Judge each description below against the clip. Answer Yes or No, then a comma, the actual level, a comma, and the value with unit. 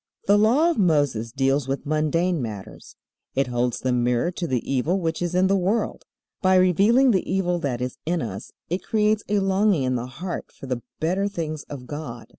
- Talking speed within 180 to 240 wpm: Yes, average, 200 wpm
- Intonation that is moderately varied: No, wide, 6.8 semitones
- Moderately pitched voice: Yes, medium, 165 Hz